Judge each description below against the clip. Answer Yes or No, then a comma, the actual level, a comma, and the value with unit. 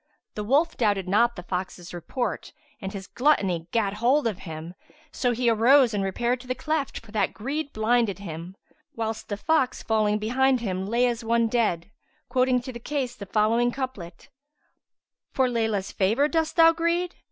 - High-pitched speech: Yes, high, 230 Hz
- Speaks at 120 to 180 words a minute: Yes, average, 175 wpm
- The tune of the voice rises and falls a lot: No, average, 4.3 semitones